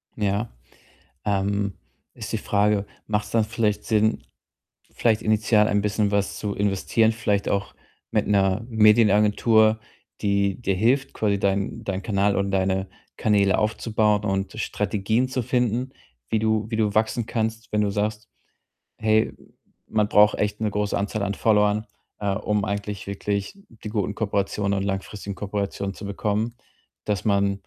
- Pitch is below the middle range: Yes, low, 105 Hz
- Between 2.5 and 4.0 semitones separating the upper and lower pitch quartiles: No, narrow, 1.5 semitones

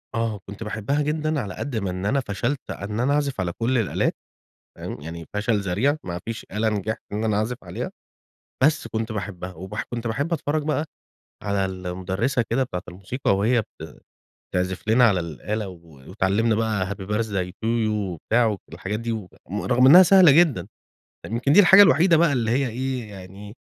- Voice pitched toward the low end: Yes, low, 110 Hz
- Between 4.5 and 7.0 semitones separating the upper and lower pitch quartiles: Yes, average, 5.2 semitones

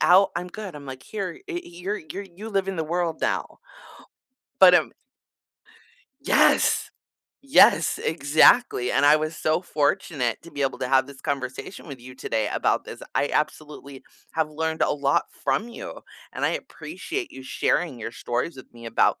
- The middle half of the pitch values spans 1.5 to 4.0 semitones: No, average, 5.0 semitones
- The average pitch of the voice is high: No, medium, 155 Hz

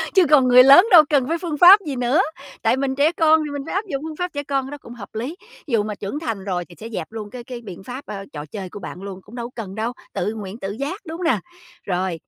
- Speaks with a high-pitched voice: Yes, very high, 250 Hz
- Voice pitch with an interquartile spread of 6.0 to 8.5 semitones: Yes, wide, 6.5 semitones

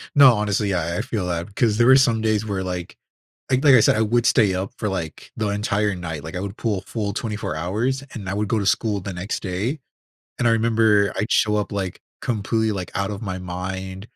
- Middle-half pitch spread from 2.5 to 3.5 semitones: Yes, average, 2.9 semitones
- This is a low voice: Yes, low, 105 Hz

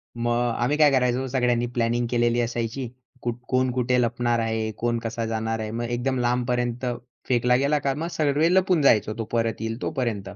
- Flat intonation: Yes, narrow, 1.9 semitones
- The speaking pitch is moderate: No, low, 120 Hz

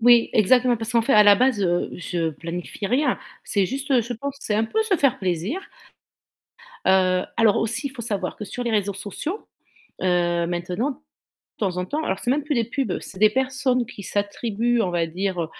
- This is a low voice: No, high, 215 Hz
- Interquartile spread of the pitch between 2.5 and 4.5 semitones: No, average, 5.3 semitones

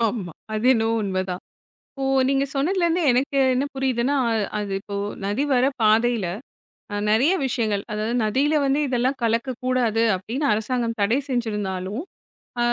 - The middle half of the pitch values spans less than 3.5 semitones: No, average, 4.0 semitones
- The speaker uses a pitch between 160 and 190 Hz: No, high, 235 Hz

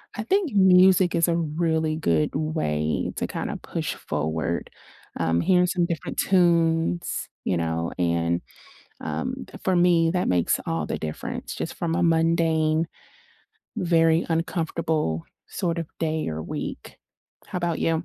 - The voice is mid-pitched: Yes, medium, 165 Hz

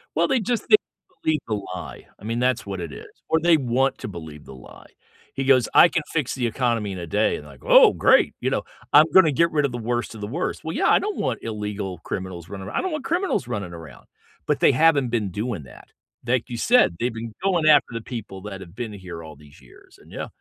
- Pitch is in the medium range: No, low, 115 Hz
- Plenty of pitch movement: Yes, wide, 7.4 semitones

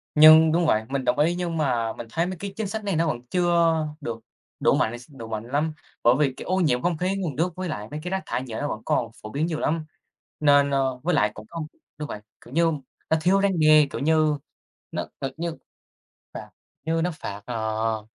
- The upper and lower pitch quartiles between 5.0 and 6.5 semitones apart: Yes, wide, 5.6 semitones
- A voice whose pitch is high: No, medium, 155 Hz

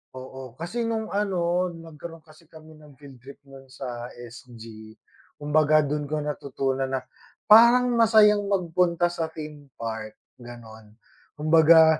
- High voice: No, medium, 150 Hz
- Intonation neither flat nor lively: Yes, average, 4.6 semitones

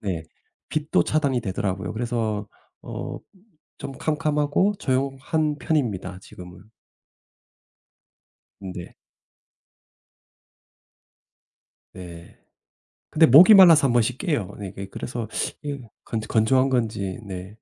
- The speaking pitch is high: No, low, 120 Hz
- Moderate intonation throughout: No, wide, 7.1 semitones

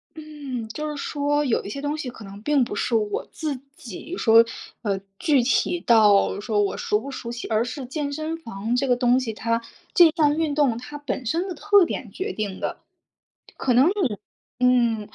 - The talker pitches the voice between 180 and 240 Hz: No, very high, 255 Hz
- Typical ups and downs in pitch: Yes, average, 4.8 semitones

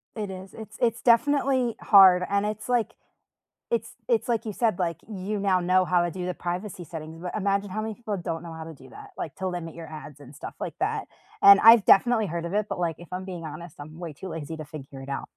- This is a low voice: No, medium, 185 Hz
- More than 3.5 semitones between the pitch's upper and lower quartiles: Yes, average, 4.6 semitones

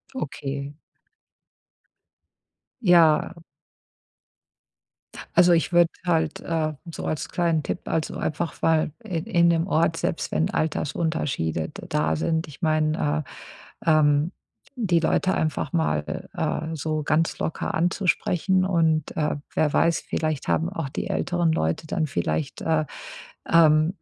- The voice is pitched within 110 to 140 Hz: No, medium, 160 Hz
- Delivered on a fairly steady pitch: Yes, narrow, 1.9 semitones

